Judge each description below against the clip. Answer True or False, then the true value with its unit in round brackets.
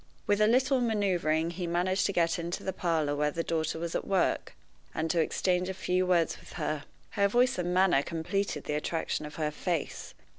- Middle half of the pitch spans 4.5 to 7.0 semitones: False (3.0 semitones)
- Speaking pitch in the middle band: True (175 Hz)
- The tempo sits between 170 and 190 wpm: False (200 wpm)